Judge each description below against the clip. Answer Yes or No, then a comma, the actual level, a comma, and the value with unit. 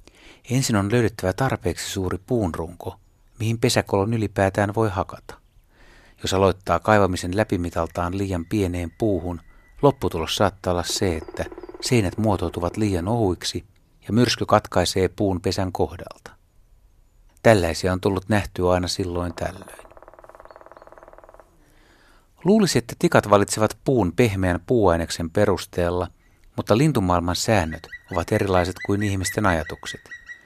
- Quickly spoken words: No, average, 110 wpm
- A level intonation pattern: No, average, 3.7 semitones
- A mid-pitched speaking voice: No, low, 100 Hz